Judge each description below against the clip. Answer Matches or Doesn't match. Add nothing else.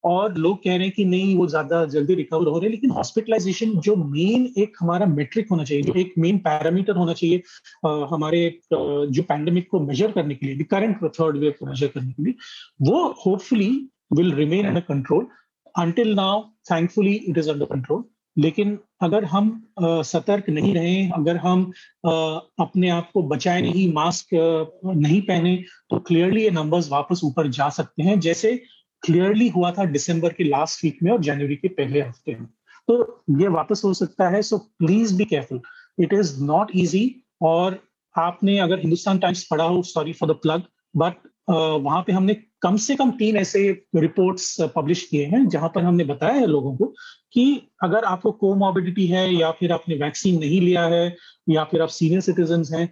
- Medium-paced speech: Matches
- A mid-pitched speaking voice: Matches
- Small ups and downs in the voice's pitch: Doesn't match